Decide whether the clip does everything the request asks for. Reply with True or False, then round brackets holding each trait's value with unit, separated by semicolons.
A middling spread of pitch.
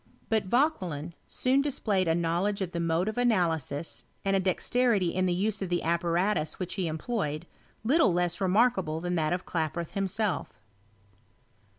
True (4.0 semitones)